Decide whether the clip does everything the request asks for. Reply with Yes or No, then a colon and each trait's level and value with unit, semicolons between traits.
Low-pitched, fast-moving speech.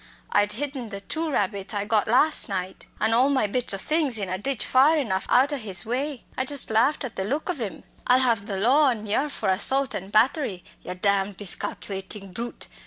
No: high, 225 Hz; fast, 215 wpm